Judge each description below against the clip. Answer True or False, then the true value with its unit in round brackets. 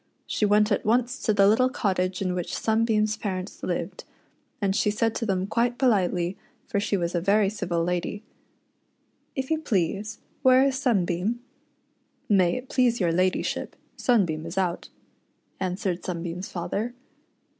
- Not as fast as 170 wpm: True (160 wpm)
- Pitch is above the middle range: True (200 Hz)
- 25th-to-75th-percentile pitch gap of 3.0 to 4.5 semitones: True (3.9 semitones)